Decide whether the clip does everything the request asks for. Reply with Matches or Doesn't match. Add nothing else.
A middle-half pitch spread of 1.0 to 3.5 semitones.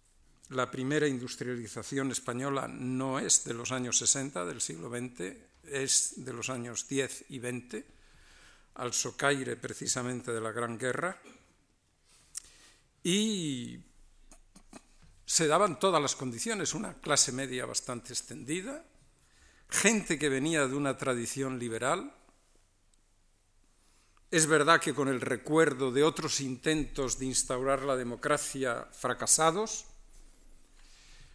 Matches